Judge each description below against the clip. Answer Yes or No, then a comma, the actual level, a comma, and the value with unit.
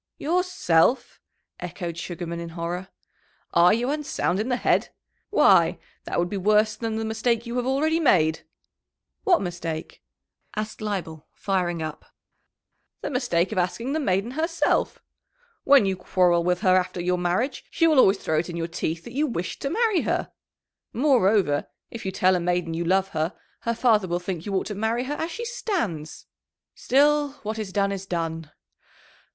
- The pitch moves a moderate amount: No, wide, 6.3 semitones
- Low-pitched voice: No, high, 195 Hz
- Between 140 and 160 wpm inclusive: No, average, 175 wpm